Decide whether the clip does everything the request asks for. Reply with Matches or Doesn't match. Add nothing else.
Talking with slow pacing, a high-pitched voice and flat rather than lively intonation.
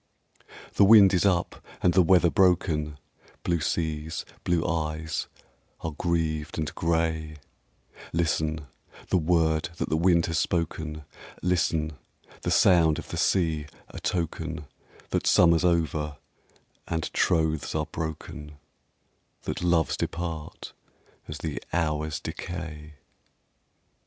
Doesn't match